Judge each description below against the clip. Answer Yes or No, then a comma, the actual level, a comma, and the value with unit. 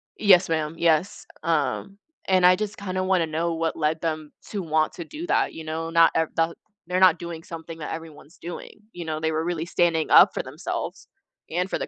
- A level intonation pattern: Yes, narrow, 2.1 semitones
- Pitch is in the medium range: Yes, medium, 165 Hz